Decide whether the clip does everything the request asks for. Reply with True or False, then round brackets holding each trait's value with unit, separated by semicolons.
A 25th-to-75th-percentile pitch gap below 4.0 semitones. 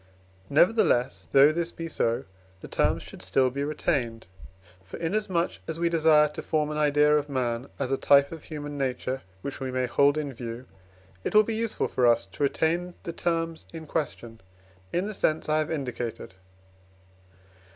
False (4.3 semitones)